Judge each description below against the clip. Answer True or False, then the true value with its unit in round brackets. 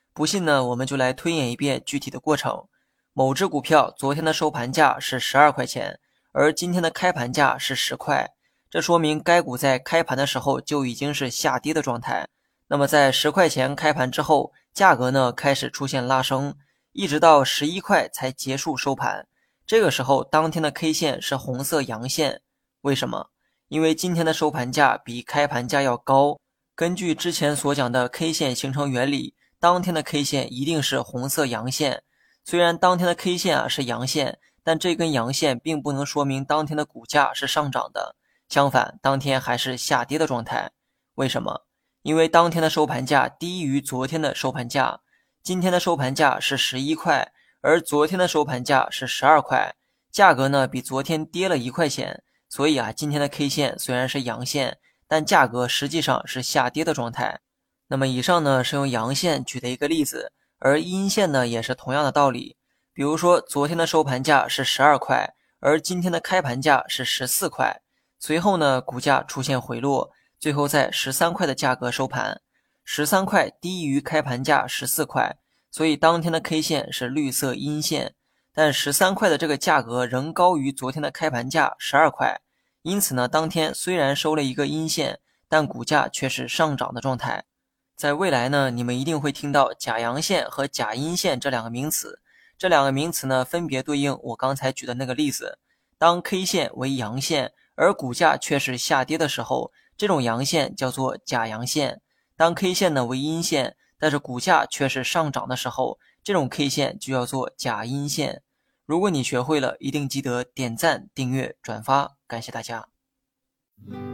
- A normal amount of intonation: True (3.3 semitones)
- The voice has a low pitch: False (145 Hz)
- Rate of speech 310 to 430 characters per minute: False (270 characters per minute)